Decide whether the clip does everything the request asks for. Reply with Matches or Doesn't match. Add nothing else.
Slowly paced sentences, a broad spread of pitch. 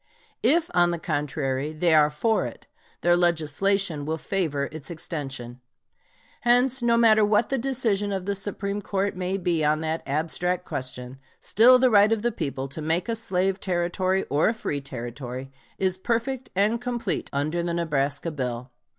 Doesn't match